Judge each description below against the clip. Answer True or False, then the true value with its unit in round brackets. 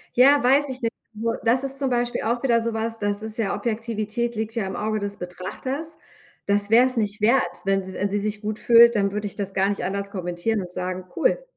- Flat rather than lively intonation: False (3.0 semitones)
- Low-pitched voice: False (220 Hz)